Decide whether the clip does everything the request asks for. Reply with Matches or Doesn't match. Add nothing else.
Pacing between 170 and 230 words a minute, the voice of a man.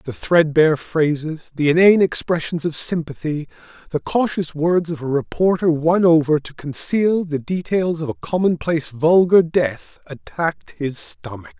Doesn't match